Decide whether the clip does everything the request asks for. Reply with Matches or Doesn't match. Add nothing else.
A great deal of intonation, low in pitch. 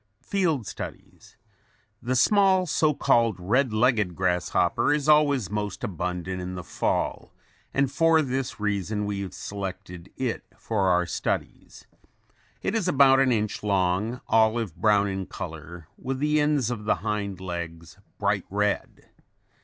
Matches